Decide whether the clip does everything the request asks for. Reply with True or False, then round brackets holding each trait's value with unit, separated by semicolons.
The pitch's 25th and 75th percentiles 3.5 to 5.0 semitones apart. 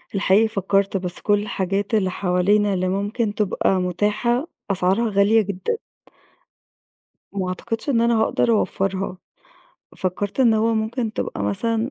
False (2.9 semitones)